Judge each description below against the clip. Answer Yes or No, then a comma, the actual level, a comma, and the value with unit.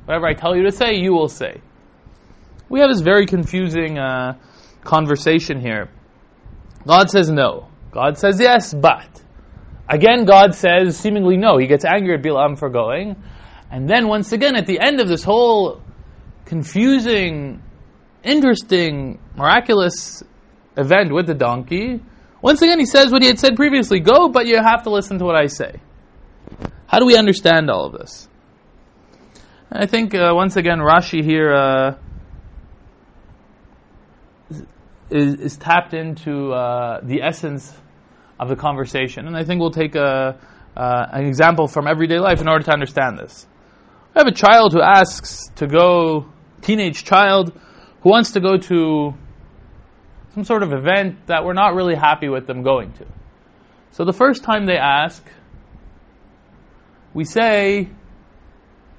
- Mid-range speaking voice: Yes, medium, 165 Hz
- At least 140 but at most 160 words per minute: Yes, average, 155 wpm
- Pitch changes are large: Yes, wide, 6.3 semitones